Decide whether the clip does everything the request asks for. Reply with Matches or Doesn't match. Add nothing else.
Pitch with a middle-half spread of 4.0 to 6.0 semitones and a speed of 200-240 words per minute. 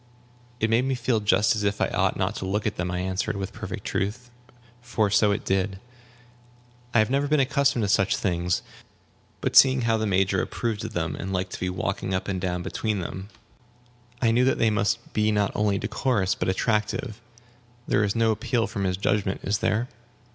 Doesn't match